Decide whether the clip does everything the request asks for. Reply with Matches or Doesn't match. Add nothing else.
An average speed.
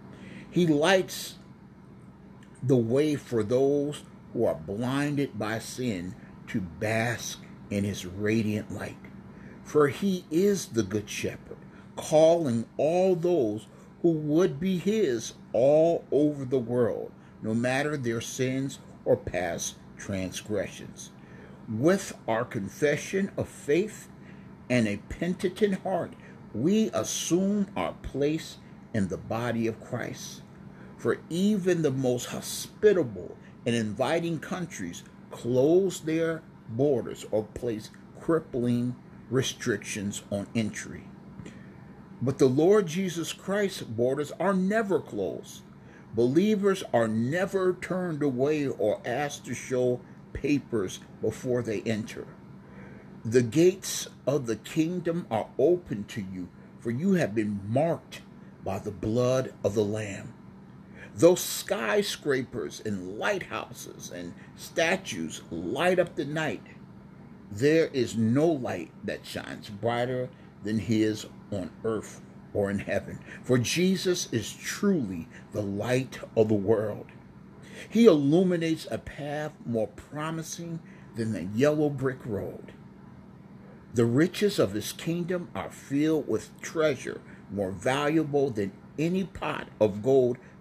Doesn't match